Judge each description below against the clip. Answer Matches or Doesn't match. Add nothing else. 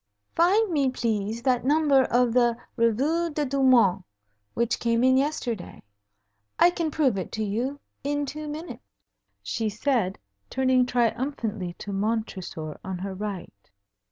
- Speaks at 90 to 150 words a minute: Matches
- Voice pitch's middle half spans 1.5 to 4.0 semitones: Doesn't match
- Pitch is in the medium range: Doesn't match